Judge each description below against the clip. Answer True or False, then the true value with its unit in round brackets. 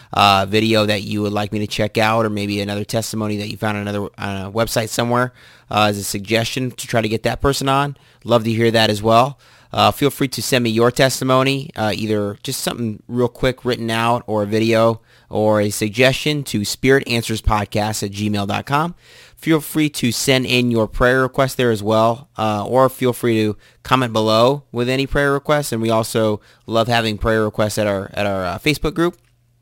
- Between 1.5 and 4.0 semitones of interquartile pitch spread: True (3.4 semitones)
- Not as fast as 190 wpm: False (205 wpm)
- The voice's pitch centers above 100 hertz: True (115 Hz)